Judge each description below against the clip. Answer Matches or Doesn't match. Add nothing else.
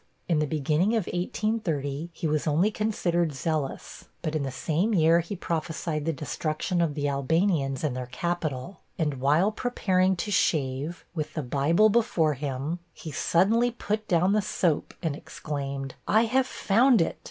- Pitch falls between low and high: Matches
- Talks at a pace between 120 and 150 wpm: Doesn't match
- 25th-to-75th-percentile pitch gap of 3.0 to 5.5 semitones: Matches